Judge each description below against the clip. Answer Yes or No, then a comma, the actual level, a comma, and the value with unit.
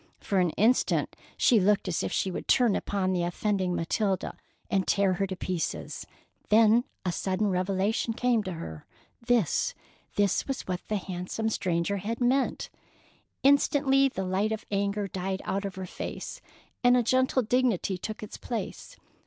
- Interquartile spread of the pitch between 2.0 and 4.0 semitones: Yes, average, 3.6 semitones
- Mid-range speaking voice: No, high, 200 Hz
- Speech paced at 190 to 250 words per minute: No, average, 160 wpm